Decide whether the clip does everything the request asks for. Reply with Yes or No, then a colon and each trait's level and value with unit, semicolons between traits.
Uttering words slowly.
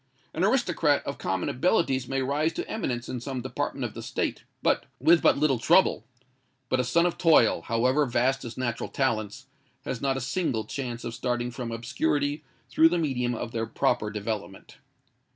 No: average, 175 wpm